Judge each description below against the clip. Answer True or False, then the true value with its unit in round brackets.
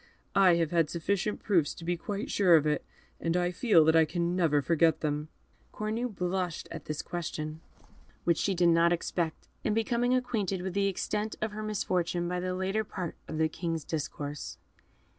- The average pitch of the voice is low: False (175 Hz)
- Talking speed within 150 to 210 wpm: True (185 wpm)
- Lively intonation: False (3.5 semitones)